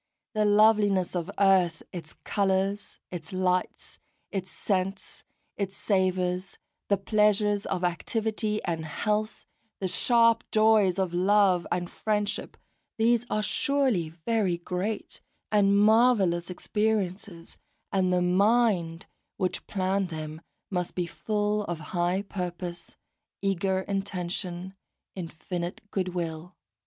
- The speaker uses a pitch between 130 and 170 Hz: No, high, 190 Hz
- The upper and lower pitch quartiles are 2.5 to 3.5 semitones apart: Yes, average, 2.8 semitones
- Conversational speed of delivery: No, slow, 110 wpm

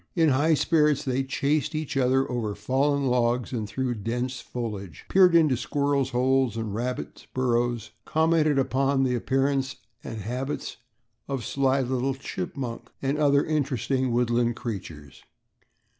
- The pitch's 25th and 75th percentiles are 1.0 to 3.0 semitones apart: Yes, average, 2.7 semitones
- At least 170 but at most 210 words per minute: No, average, 145 wpm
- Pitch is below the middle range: Yes, low, 130 Hz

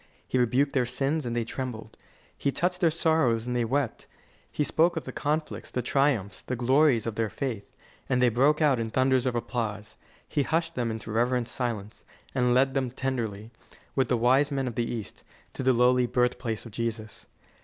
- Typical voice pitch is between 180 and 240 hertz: No, low, 125 Hz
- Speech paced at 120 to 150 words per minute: No, average, 195 wpm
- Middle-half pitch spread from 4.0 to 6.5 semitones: No, average, 2.9 semitones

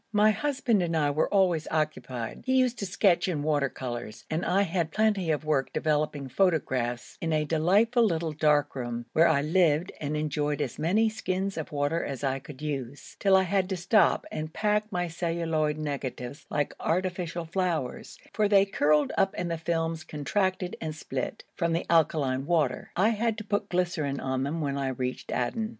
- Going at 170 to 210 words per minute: Yes, average, 185 wpm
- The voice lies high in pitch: No, medium, 160 Hz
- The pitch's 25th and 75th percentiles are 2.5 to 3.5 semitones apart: No, average, 4.5 semitones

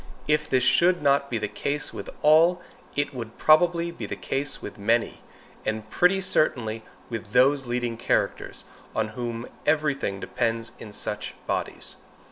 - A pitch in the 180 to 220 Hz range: No, low, 130 Hz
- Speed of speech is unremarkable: Yes, average, 155 wpm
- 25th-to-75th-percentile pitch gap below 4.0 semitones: No, average, 5.0 semitones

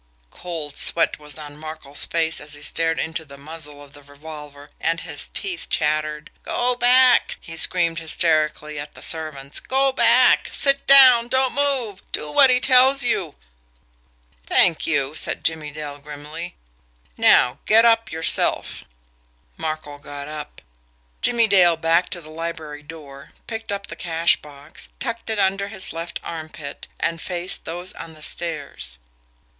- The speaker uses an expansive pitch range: No, average, 4.9 semitones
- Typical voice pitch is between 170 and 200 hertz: No, medium, 160 Hz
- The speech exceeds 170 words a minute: No, average, 155 wpm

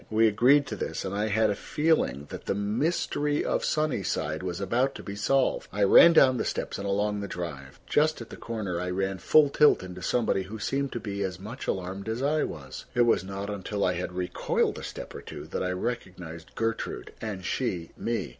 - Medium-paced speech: No, fast, 215 wpm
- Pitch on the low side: Yes, low, 100 Hz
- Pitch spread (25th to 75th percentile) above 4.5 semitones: Yes, average, 4.9 semitones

